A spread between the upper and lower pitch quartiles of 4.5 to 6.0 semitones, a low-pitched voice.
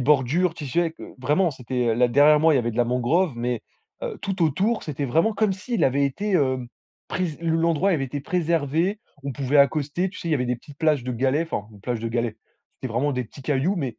No: average, 5.0 semitones; medium, 145 Hz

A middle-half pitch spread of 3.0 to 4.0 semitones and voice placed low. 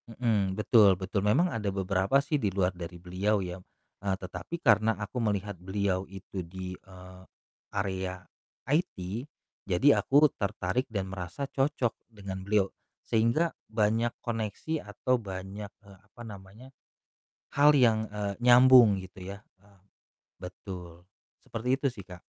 Yes: average, 3.5 semitones; low, 100 Hz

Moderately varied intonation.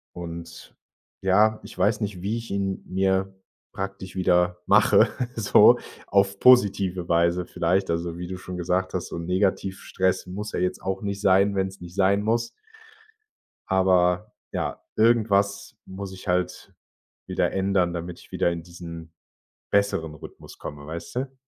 No: narrow, 2.1 semitones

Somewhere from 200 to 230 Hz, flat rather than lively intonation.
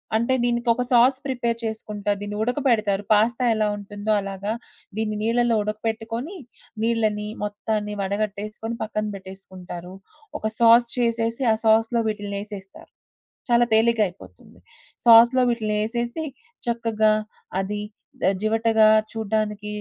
Yes: high, 220 Hz; narrow, 2.0 semitones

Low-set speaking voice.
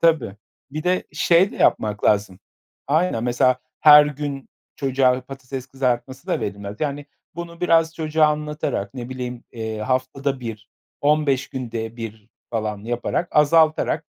Yes: low, 130 Hz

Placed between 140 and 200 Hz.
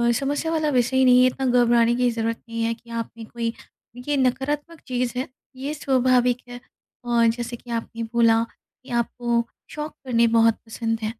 No: high, 240 Hz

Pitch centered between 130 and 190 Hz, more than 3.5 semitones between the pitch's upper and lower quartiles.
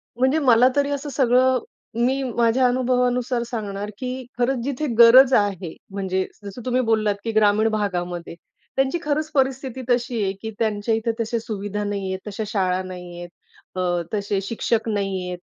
No: high, 225 Hz; average, 4.2 semitones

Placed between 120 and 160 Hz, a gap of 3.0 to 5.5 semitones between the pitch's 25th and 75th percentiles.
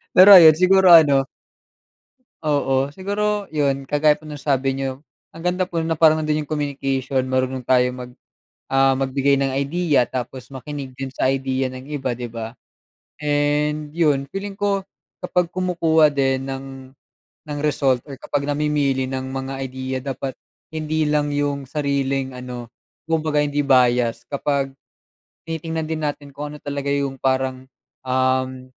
No: medium, 140 Hz; narrow, 2.5 semitones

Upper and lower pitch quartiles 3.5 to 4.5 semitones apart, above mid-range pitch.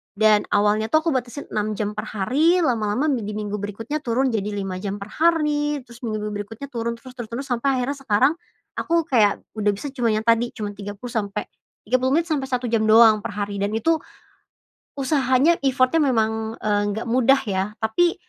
Yes: average, 4.2 semitones; high, 230 Hz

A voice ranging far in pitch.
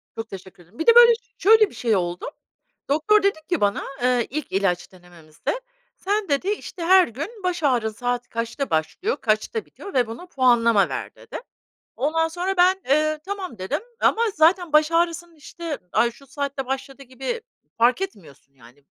Yes: wide, 8.0 semitones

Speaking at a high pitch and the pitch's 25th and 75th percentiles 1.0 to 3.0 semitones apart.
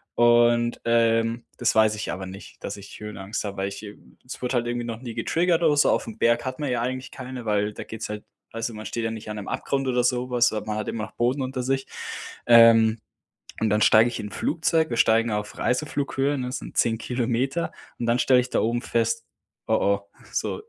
No: low, 115 Hz; average, 2.7 semitones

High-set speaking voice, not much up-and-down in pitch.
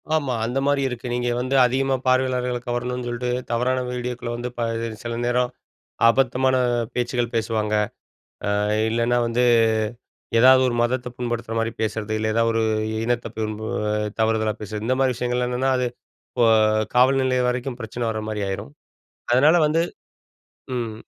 No: low, 120 Hz; narrow, 1.9 semitones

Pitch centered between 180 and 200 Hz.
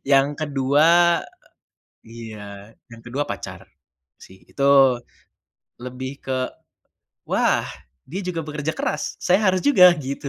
No: low, 135 Hz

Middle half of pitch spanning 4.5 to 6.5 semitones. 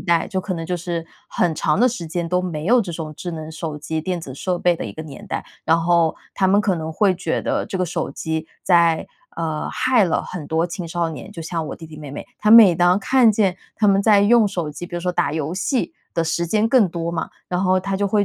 No: average, 3.2 semitones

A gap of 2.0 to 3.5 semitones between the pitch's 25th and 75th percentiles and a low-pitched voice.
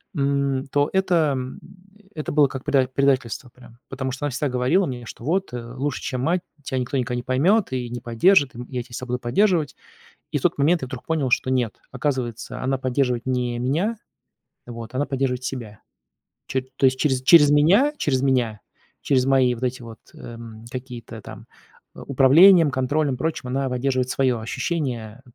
Yes: average, 2.9 semitones; low, 130 Hz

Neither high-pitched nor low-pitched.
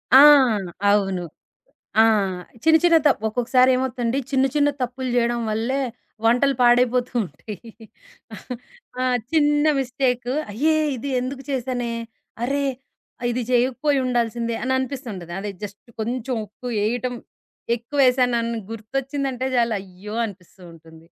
No: high, 245 Hz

